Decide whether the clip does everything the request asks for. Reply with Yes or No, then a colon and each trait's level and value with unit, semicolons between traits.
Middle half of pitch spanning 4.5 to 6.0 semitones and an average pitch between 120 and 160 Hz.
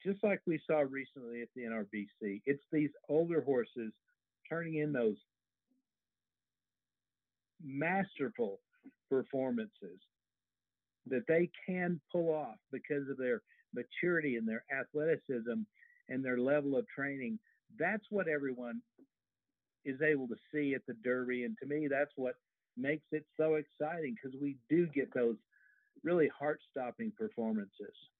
Yes: average, 5.0 semitones; medium, 140 Hz